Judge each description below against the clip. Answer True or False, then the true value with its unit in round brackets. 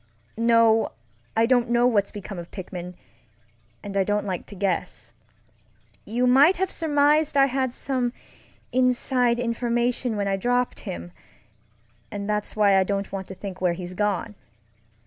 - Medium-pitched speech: False (215 Hz)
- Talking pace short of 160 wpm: True (145 wpm)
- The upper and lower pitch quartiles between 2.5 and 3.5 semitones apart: False (4.5 semitones)